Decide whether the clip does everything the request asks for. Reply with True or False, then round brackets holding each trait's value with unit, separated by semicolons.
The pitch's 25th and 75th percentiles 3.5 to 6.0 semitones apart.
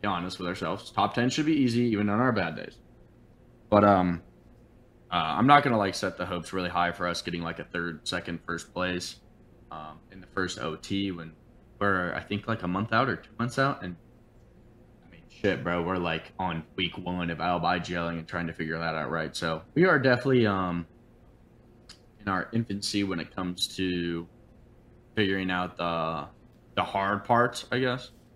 True (5.2 semitones)